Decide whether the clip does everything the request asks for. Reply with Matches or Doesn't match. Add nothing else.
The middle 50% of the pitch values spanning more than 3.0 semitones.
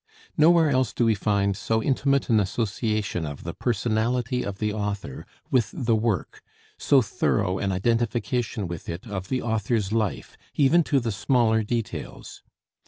Matches